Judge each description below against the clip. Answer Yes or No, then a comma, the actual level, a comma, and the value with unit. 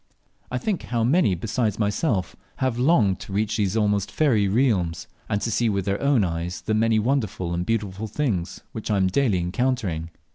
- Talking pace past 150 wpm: Yes, average, 190 wpm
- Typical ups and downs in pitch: Yes, average, 4.4 semitones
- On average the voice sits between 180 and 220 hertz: No, low, 105 Hz